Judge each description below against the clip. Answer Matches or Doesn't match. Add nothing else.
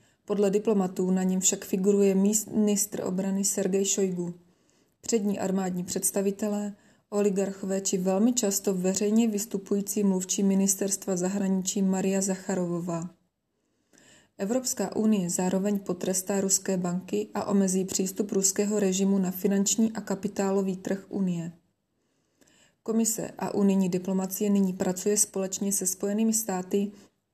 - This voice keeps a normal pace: Doesn't match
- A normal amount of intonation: Doesn't match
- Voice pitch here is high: Matches